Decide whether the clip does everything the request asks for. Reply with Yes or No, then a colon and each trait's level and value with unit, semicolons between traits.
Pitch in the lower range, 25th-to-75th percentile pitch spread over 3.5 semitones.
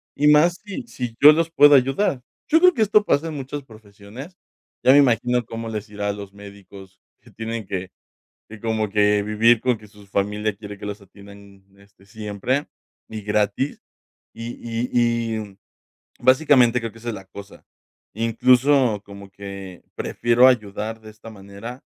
Yes: low, 110 Hz; average, 4.0 semitones